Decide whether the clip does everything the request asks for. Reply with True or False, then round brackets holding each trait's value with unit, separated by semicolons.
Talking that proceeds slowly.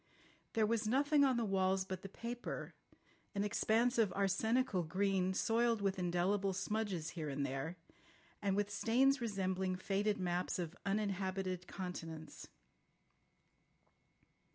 True (125 wpm)